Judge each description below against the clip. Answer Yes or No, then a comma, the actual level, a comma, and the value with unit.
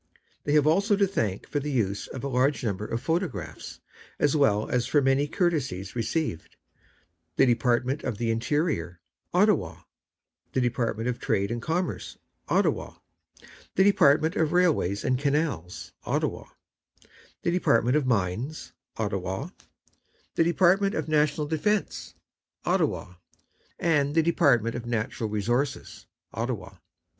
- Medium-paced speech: No, slow, 130 wpm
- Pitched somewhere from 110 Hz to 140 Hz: Yes, low, 135 Hz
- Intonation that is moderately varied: No, wide, 5.7 semitones